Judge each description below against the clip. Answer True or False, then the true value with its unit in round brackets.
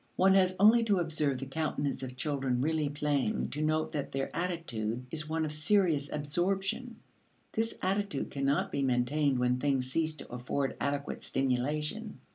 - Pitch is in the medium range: True (150 Hz)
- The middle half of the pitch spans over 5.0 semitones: False (4.5 semitones)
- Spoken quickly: False (160 wpm)